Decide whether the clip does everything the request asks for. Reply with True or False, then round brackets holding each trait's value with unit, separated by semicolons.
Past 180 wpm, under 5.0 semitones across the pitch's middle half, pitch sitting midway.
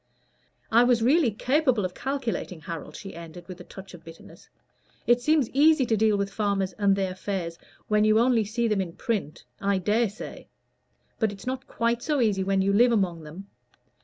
False (190 wpm; 3.9 semitones; 210 Hz)